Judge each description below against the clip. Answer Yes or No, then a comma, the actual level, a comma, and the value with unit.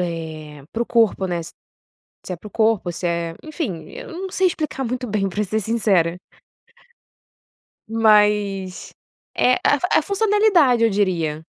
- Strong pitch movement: Yes, wide, 6.1 semitones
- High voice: Yes, high, 210 Hz